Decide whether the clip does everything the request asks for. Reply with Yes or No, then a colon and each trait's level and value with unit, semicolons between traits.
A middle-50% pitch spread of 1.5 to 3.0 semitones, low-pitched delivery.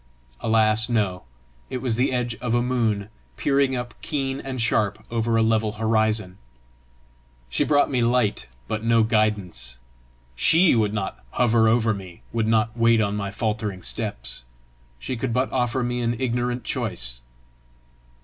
Yes: narrow, 2.5 semitones; low, 115 Hz